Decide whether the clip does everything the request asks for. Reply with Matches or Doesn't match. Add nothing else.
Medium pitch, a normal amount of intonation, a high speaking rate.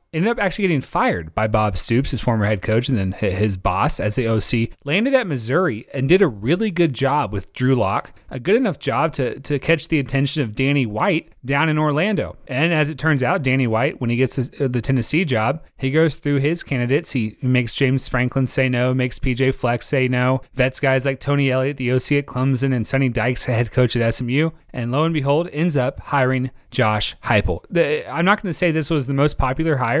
Doesn't match